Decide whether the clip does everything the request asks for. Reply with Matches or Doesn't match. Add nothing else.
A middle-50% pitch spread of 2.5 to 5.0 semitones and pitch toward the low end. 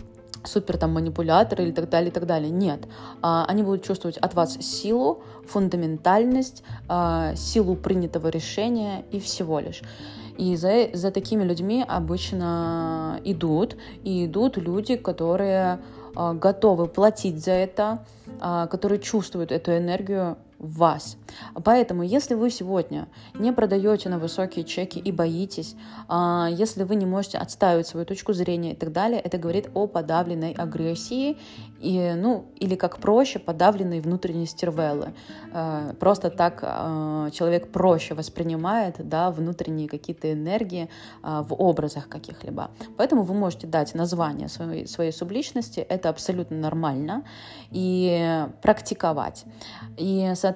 Doesn't match